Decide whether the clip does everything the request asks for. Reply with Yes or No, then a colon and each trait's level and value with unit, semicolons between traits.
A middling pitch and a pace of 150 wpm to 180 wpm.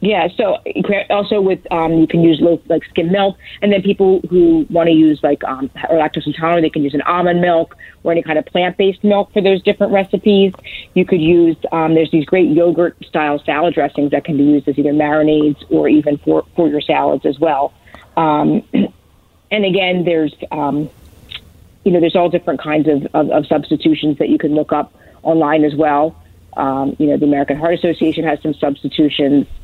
No: medium, 160 Hz; average, 200 wpm